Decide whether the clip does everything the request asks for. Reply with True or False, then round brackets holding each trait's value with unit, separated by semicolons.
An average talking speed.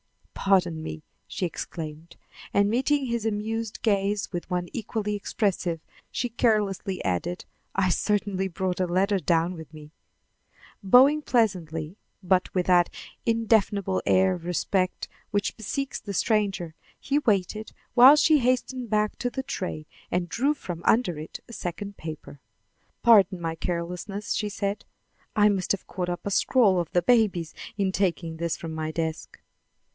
True (150 wpm)